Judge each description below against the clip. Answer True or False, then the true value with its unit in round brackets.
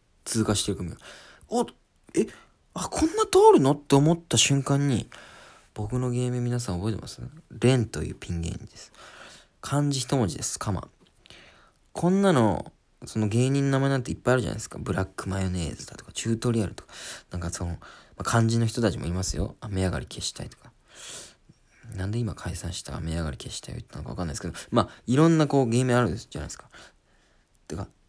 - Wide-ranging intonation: True (6.2 semitones)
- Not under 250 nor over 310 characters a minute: False (395 characters per minute)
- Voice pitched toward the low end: True (115 Hz)